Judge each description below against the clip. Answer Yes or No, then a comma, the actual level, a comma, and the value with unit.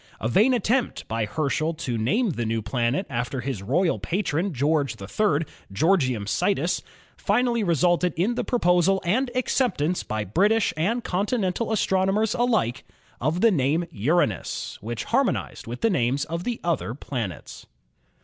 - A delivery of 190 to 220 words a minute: No, average, 150 wpm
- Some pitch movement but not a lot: No, wide, 8.6 semitones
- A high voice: No, medium, 170 Hz